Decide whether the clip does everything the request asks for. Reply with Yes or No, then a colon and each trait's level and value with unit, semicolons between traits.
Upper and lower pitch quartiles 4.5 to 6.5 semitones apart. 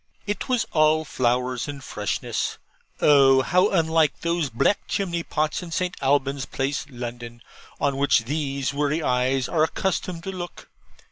No: average, 4.1 semitones